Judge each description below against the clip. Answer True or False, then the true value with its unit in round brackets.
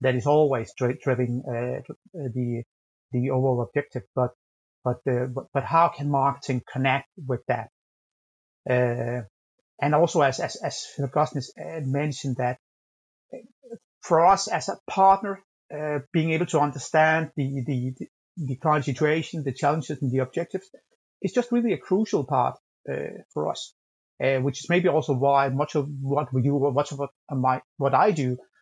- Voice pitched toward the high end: False (140 Hz)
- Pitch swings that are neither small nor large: True (3.6 semitones)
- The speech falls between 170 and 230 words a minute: False (150 wpm)